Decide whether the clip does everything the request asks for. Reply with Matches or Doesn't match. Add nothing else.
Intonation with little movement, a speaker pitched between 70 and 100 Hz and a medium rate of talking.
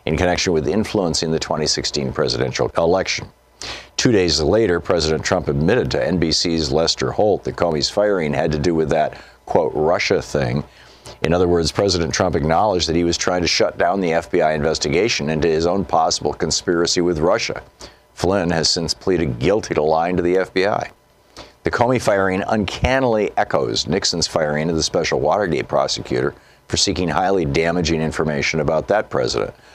Matches